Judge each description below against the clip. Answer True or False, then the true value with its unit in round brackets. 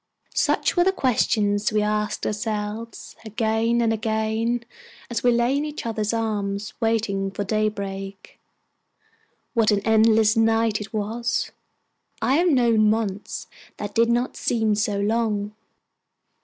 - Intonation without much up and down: True (1.8 semitones)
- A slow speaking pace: True (130 wpm)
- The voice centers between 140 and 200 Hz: False (220 Hz)